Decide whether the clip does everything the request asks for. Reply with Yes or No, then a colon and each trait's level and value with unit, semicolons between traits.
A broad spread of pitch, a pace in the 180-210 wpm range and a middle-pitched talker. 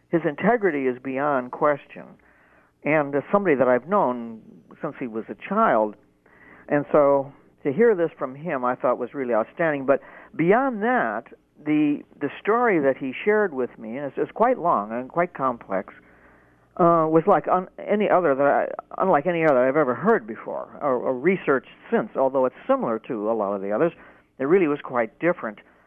Yes: wide, 6.1 semitones; average, 185 wpm; medium, 145 Hz